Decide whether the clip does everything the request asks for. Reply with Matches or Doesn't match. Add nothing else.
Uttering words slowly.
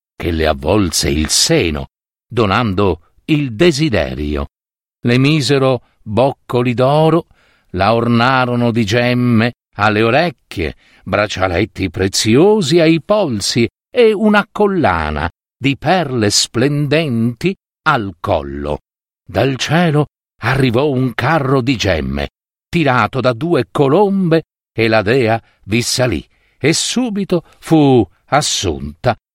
Matches